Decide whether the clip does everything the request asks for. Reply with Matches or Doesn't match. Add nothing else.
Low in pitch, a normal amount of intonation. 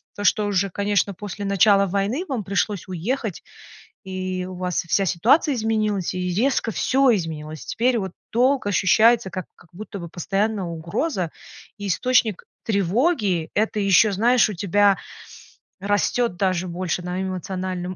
Doesn't match